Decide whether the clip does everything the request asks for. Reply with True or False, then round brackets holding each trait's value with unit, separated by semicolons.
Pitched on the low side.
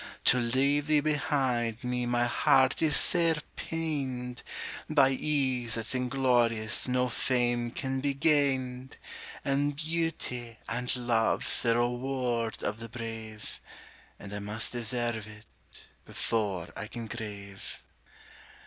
True (125 Hz)